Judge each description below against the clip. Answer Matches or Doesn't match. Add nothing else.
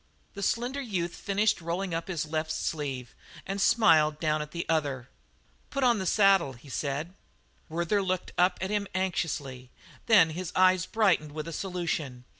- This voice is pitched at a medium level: Matches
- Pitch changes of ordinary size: Matches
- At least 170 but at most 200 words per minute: Doesn't match